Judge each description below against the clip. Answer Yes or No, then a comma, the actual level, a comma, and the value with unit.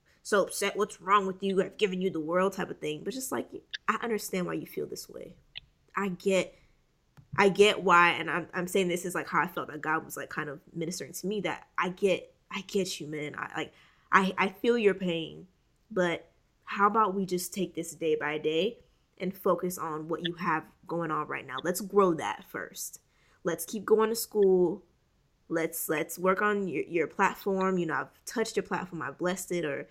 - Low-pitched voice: No, medium, 185 Hz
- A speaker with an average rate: No, fast, 215 wpm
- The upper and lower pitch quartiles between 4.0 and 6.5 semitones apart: No, average, 3.2 semitones